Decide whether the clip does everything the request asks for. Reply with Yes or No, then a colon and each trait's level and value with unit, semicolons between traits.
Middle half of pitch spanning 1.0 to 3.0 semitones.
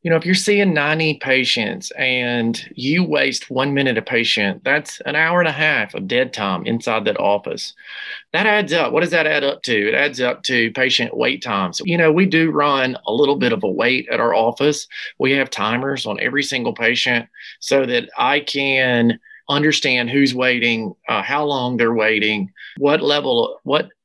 No: average, 4.2 semitones